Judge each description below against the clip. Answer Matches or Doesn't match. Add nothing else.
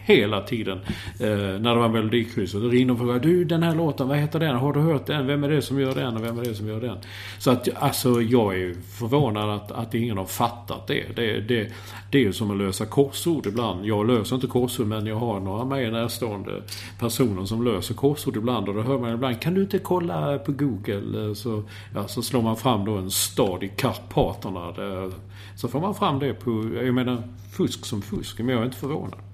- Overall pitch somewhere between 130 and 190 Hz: Doesn't match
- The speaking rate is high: Matches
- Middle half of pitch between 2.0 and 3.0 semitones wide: Doesn't match